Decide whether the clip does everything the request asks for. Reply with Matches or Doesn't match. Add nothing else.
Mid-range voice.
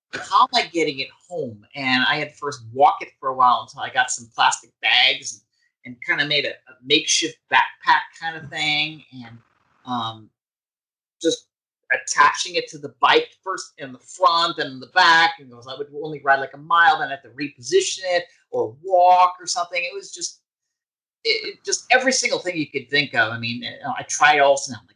Matches